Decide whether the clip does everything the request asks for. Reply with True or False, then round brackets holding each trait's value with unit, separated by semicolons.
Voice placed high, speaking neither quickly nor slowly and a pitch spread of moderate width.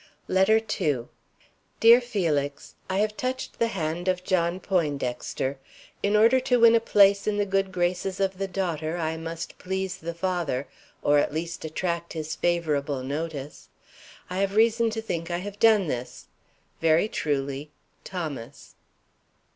False (175 Hz; 150 wpm; 4.3 semitones)